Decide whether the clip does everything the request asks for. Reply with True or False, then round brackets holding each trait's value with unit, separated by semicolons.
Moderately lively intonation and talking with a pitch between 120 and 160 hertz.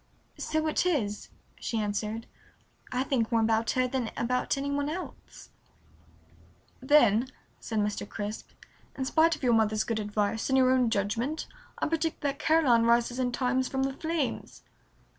False (4.2 semitones; 250 Hz)